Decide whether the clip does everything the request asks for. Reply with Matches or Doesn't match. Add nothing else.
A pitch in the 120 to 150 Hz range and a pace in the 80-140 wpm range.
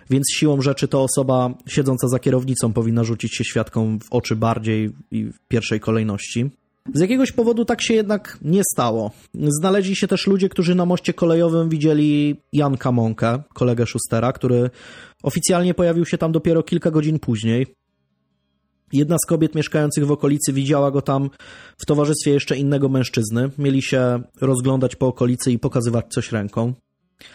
Doesn't match